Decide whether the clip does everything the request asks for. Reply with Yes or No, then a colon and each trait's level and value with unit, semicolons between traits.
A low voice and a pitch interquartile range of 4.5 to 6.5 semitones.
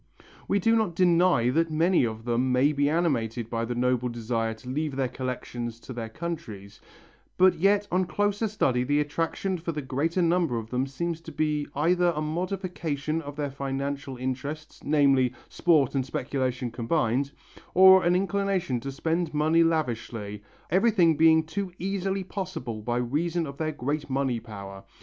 No: medium, 150 Hz; wide, 5.4 semitones